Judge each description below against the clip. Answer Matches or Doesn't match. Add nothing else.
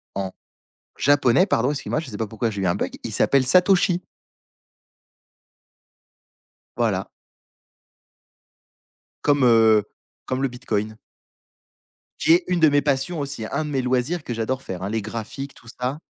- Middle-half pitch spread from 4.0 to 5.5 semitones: Matches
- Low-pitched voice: Matches